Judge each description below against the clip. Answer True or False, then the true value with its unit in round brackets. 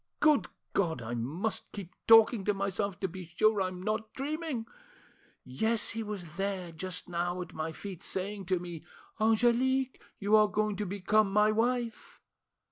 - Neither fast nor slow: True (160 wpm)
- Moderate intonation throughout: True (3.6 semitones)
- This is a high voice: True (200 Hz)